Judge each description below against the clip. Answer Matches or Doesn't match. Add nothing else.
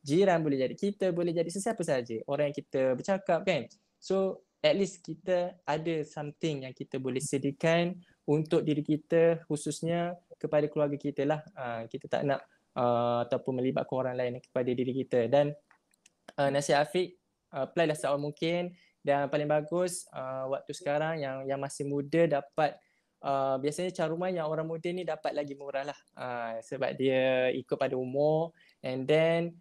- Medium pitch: Matches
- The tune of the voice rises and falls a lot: Doesn't match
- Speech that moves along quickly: Matches